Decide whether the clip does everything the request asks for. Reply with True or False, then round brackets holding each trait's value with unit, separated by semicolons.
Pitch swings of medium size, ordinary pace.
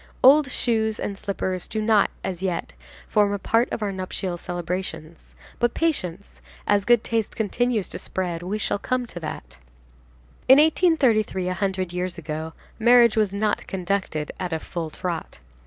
True (4.0 semitones; 160 wpm)